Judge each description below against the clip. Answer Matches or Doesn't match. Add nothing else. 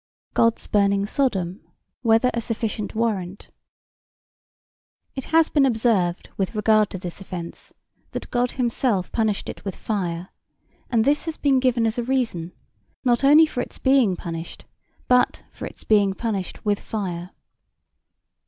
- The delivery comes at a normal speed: Matches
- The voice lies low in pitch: Doesn't match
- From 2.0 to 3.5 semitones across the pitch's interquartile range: Doesn't match